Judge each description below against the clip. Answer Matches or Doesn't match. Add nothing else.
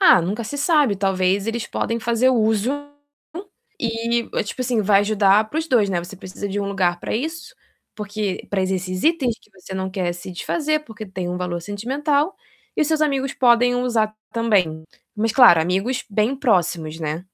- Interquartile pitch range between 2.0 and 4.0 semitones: Doesn't match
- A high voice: Matches